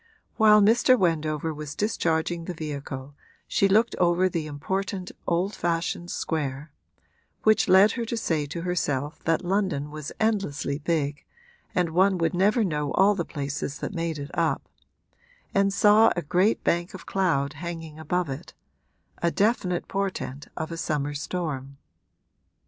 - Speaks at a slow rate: No, average, 150 wpm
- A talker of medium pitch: Yes, medium, 170 Hz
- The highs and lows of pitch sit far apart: No, average, 4.4 semitones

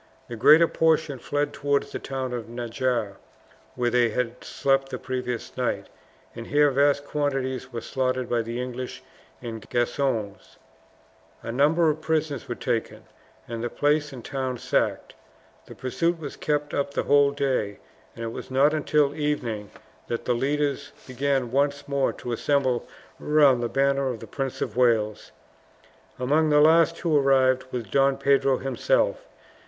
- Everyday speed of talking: Yes, average, 160 wpm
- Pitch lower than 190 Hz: Yes, low, 135 Hz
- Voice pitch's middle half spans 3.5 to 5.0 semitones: No, average, 3.1 semitones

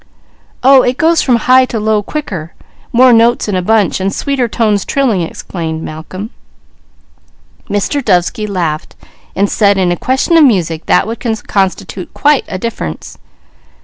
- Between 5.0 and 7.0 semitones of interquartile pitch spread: Yes, wide, 5.6 semitones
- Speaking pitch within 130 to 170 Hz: No, high, 210 Hz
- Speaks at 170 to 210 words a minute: No, average, 145 wpm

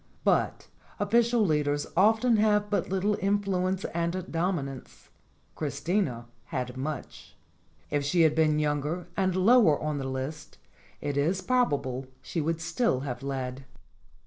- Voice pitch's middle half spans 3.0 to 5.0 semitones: No, wide, 5.5 semitones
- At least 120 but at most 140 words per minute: Yes, slow, 135 wpm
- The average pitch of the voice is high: No, medium, 160 Hz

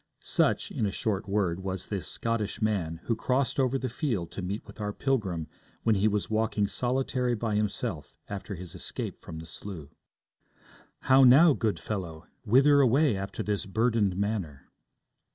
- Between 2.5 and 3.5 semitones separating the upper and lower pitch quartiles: No, average, 4.3 semitones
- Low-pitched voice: Yes, low, 105 Hz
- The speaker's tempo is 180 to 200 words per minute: No, average, 165 wpm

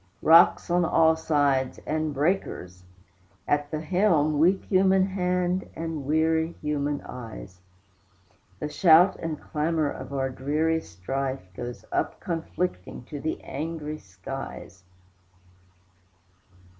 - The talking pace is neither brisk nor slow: No, slow, 110 wpm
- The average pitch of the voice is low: No, medium, 155 Hz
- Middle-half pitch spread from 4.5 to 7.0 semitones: No, average, 3.3 semitones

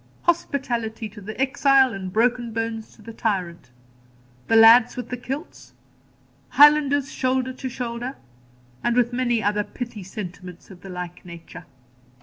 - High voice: Yes, high, 230 Hz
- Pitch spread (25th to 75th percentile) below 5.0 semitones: Yes, average, 3.8 semitones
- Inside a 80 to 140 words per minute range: Yes, slow, 135 wpm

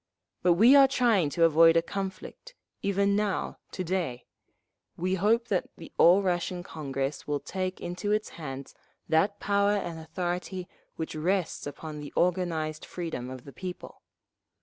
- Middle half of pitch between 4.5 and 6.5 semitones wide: No, average, 3.8 semitones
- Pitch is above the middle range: No, medium, 175 Hz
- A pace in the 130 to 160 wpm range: Yes, average, 150 wpm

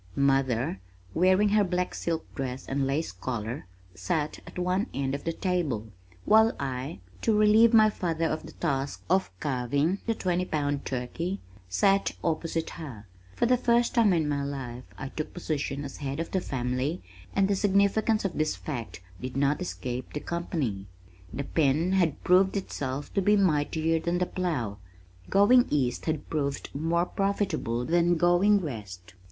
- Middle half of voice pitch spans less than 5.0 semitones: No, wide, 5.6 semitones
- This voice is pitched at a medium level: Yes, medium, 160 Hz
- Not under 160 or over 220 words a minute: Yes, average, 165 wpm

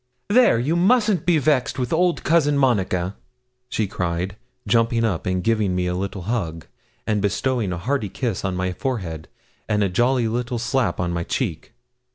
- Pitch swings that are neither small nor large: No, wide, 6.3 semitones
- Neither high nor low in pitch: No, low, 115 Hz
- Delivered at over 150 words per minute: Yes, average, 175 wpm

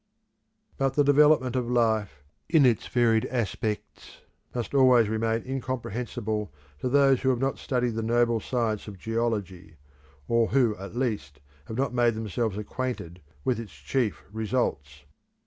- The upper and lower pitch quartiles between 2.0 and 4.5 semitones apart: Yes, average, 3.2 semitones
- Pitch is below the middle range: Yes, low, 115 Hz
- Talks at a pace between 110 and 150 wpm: Yes, average, 145 wpm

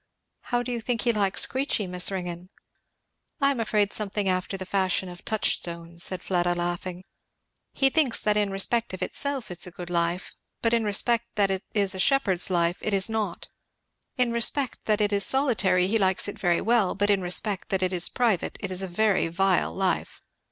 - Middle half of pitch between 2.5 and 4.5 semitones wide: Yes, average, 3.7 semitones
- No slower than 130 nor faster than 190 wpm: No, average, 200 wpm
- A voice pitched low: No, high, 195 Hz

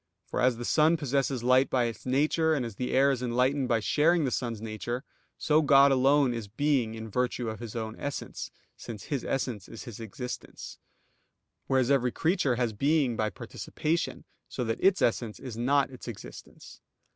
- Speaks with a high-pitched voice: No, low, 125 Hz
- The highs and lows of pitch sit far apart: No, average, 3.3 semitones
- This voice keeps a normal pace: Yes, average, 180 wpm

